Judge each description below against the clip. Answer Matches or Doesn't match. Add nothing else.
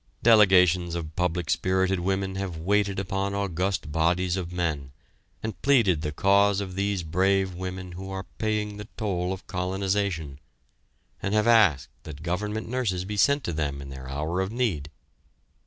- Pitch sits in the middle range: Doesn't match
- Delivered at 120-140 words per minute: Doesn't match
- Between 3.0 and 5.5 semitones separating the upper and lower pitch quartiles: Doesn't match